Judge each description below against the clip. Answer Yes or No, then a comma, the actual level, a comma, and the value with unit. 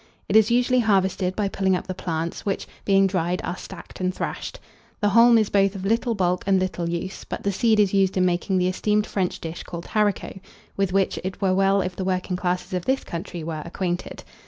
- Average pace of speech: No, fast, 220 wpm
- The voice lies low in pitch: No, high, 190 Hz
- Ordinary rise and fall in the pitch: No, narrow, 1.9 semitones